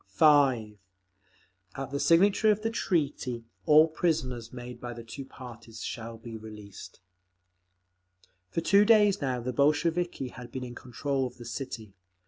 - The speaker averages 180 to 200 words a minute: No, average, 145 wpm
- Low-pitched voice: Yes, low, 130 Hz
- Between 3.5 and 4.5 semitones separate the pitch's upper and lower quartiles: No, average, 5.2 semitones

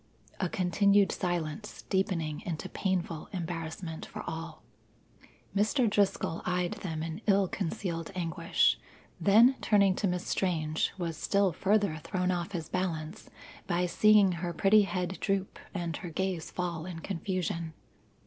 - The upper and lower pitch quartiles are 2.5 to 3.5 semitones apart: Yes, average, 3.0 semitones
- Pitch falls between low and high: Yes, medium, 180 Hz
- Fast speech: No, slow, 135 wpm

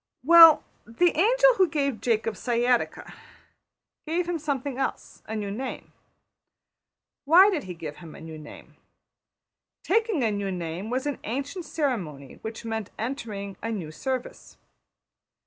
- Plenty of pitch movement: Yes, wide, 7.3 semitones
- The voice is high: Yes, high, 245 Hz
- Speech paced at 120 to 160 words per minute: Yes, average, 140 wpm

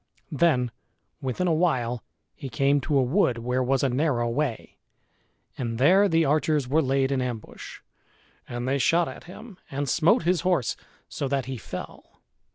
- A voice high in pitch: No, low, 135 Hz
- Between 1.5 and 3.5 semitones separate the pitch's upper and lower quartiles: No, average, 4.2 semitones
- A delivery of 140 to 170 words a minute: Yes, average, 165 wpm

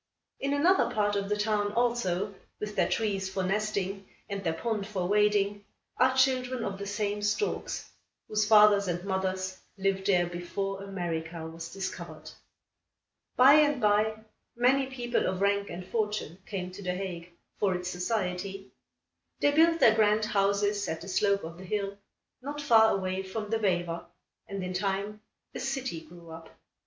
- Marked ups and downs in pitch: No, narrow, 2.6 semitones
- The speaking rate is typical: Yes, average, 165 wpm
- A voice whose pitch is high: Yes, high, 200 Hz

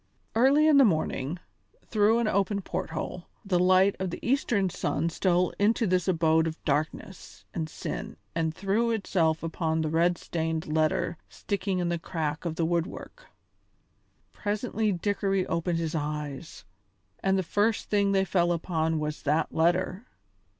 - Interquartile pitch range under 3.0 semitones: No, average, 3.7 semitones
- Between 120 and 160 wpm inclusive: Yes, average, 155 wpm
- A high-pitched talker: No, medium, 175 Hz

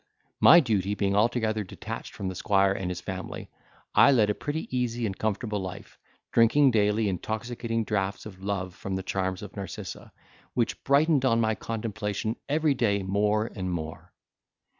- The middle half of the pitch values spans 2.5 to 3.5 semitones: Yes, average, 3.1 semitones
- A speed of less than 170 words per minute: Yes, average, 160 wpm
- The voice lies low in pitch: Yes, low, 105 Hz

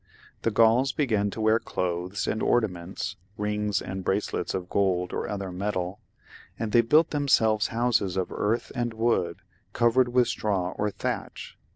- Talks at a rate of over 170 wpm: No, average, 160 wpm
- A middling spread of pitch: Yes, average, 3.7 semitones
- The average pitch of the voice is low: Yes, low, 105 Hz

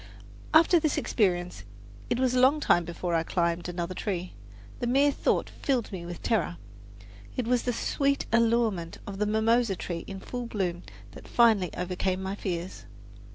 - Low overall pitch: No, high, 200 Hz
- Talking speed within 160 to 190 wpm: Yes, average, 165 wpm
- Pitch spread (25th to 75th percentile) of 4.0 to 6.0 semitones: Yes, wide, 5.5 semitones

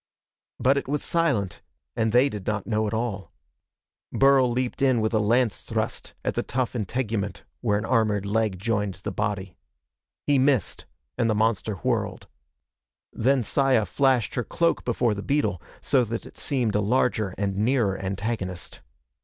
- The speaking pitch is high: No, low, 110 Hz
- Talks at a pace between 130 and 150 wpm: No, average, 160 wpm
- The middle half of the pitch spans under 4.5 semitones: Yes, average, 3.8 semitones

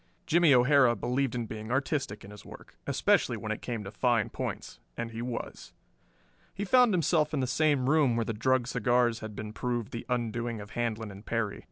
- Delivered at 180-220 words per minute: Yes, average, 200 wpm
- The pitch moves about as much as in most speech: Yes, average, 3.3 semitones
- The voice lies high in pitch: No, low, 120 Hz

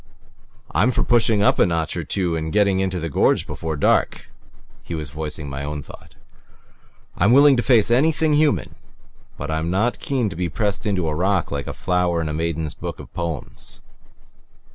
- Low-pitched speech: Yes, very low, 90 Hz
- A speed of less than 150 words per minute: No, average, 185 wpm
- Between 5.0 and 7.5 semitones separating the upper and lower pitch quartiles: Yes, average, 5.3 semitones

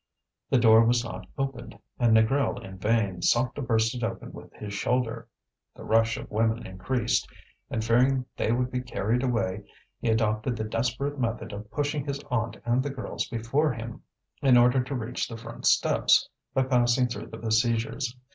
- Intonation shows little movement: Yes, narrow, 2.2 semitones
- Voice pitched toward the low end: Yes, low, 120 Hz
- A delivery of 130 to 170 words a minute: No, average, 180 wpm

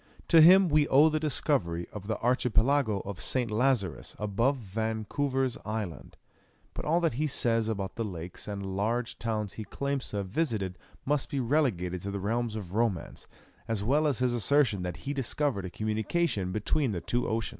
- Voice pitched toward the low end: Yes, low, 115 Hz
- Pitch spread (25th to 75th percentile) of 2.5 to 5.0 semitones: No, wide, 5.6 semitones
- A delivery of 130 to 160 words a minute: No, average, 180 wpm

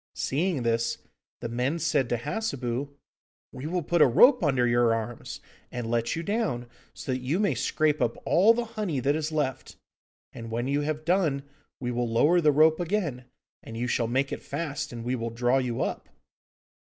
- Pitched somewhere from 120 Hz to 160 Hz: Yes, low, 135 Hz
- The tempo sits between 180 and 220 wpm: Yes, average, 190 wpm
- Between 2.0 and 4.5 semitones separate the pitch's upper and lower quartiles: No, average, 4.9 semitones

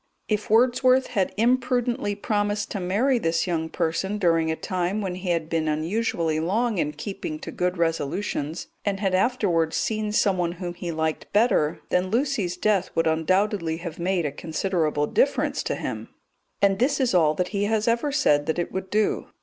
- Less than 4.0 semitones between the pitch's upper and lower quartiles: No, average, 4.4 semitones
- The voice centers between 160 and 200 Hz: Yes, medium, 185 Hz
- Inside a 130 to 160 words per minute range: No, average, 180 wpm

